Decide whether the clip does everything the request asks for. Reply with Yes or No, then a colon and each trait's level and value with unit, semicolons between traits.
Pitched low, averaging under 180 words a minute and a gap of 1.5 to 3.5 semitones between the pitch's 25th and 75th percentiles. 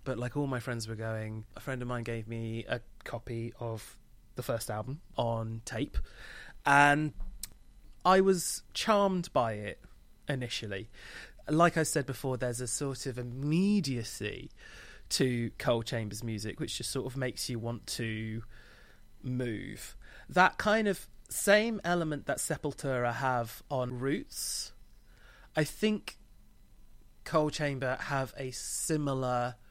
No: low, 125 Hz; slow, 135 wpm; average, 4.3 semitones